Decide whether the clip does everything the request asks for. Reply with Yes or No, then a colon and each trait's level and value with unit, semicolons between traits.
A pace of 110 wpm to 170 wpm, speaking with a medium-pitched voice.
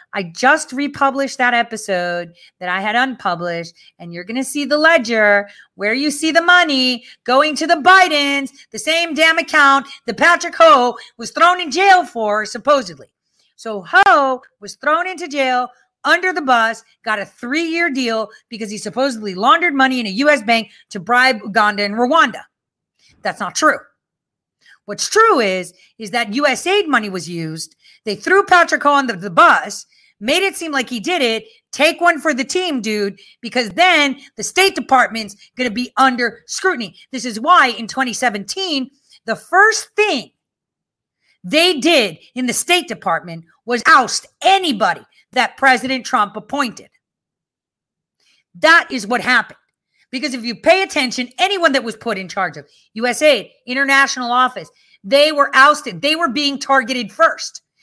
No: average, 160 wpm; very high, 265 Hz